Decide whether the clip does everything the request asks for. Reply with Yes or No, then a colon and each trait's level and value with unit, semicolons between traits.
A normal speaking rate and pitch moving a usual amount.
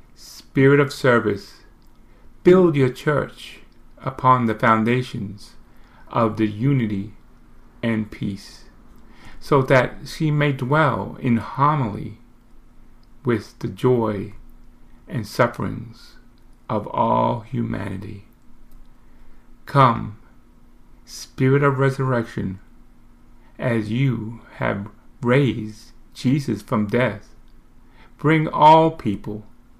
No: slow, 85 wpm; average, 3.1 semitones